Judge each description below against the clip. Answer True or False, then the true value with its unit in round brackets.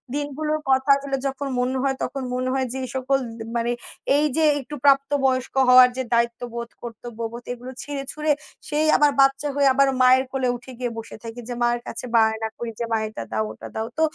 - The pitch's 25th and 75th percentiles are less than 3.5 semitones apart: True (2.7 semitones)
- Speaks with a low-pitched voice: False (255 Hz)